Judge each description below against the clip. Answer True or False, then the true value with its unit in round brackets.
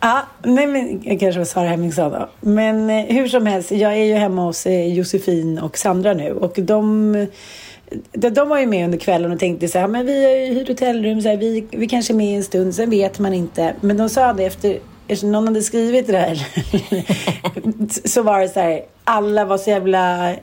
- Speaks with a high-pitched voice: True (205 Hz)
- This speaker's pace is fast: True (225 wpm)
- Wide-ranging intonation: False (3.2 semitones)